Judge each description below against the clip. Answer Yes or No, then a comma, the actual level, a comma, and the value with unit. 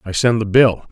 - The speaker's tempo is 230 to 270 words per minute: Yes, fast, 260 wpm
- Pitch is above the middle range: No, low, 110 Hz